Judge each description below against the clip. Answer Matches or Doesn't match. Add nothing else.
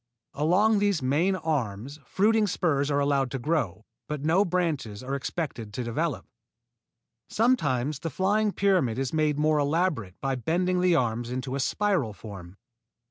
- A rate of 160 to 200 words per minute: Doesn't match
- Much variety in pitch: Matches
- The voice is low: Doesn't match